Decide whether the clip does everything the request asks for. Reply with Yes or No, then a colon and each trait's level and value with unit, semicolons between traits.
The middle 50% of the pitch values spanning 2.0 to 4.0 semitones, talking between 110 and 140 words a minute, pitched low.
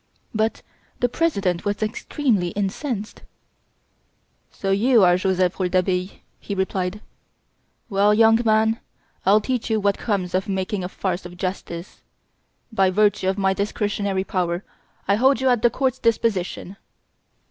No: average, 3.0 semitones; slow, 135 wpm; high, 200 Hz